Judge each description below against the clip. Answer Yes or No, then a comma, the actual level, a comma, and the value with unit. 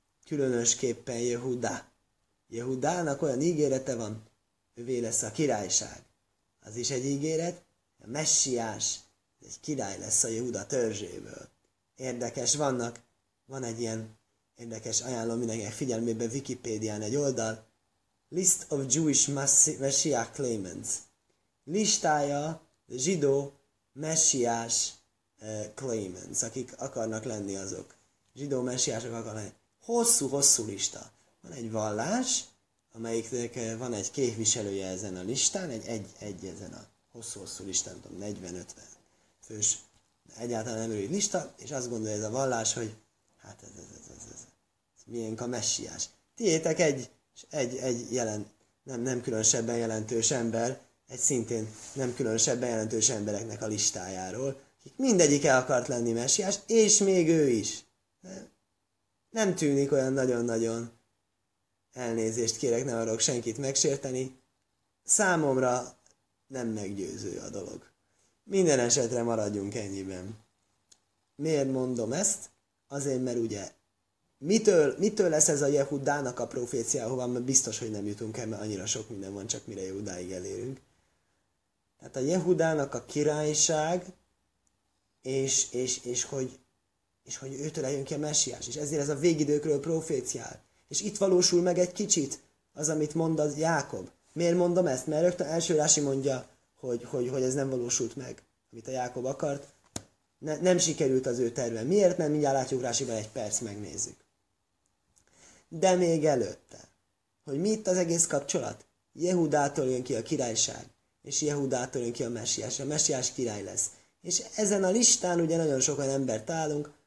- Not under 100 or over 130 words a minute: No, average, 140 wpm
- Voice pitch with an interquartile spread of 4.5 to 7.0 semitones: Yes, average, 5.0 semitones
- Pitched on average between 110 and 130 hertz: Yes, low, 125 Hz